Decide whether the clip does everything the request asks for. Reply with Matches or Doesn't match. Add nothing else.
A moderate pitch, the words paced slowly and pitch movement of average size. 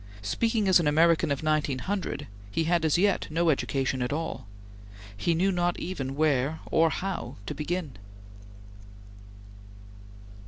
Matches